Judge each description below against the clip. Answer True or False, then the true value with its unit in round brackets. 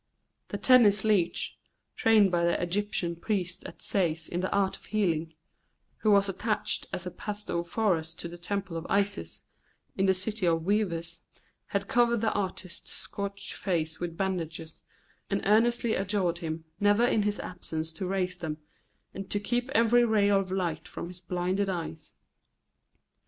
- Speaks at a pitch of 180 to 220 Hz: True (190 Hz)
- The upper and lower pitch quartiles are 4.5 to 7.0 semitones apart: False (3.3 semitones)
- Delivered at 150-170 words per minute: True (155 wpm)